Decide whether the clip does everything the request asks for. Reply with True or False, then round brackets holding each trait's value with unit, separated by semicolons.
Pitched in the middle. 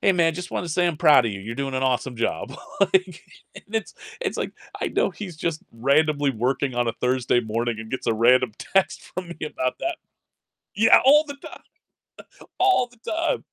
True (150 Hz)